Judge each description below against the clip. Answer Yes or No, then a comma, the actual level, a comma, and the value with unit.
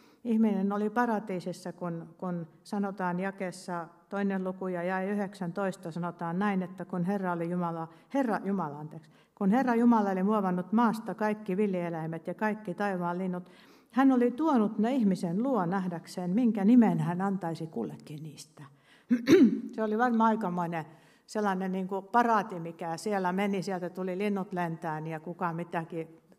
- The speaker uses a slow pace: No, average, 150 wpm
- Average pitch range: Yes, average, 3.5 semitones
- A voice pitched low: No, medium, 185 Hz